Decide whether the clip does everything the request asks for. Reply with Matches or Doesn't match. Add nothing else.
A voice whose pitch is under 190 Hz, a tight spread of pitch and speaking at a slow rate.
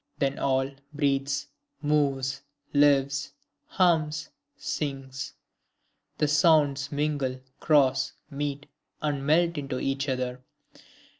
Matches